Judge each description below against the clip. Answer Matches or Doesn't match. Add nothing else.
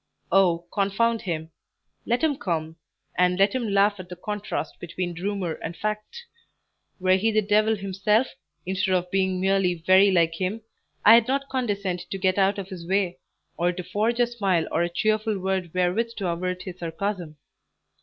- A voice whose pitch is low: Doesn't match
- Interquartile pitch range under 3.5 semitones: Matches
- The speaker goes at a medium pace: Matches